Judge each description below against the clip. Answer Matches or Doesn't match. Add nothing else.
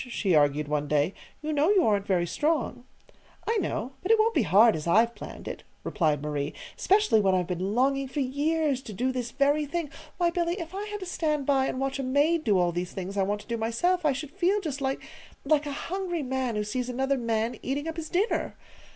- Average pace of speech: Doesn't match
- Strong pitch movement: Matches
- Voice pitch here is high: Matches